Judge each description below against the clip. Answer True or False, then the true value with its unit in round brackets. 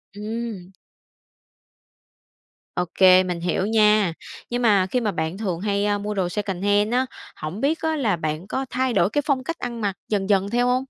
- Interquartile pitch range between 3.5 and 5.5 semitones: True (4.2 semitones)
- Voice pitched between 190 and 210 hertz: True (205 Hz)